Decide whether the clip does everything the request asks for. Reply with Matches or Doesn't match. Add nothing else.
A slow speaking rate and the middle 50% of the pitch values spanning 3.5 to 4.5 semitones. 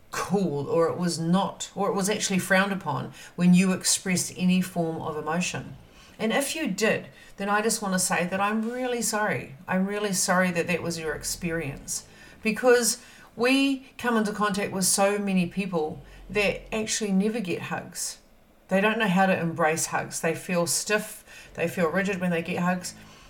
Doesn't match